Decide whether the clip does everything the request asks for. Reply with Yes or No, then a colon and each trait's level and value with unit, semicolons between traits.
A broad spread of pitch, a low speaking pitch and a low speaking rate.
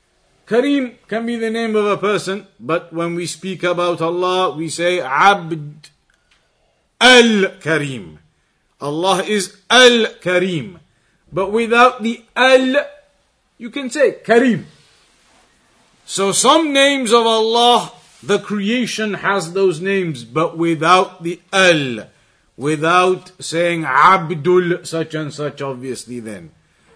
No: wide, 5.8 semitones; medium, 185 Hz; slow, 115 wpm